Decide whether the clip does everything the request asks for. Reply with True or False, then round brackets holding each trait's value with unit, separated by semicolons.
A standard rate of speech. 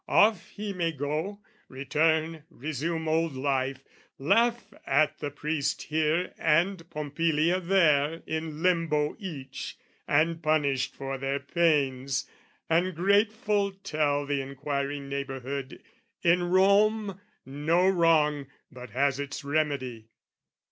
False (110 wpm)